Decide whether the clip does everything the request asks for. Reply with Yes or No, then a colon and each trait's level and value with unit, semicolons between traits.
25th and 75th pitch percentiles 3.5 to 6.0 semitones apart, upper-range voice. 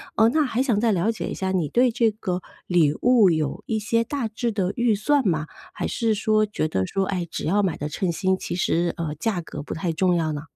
Yes: average, 5.0 semitones; high, 195 Hz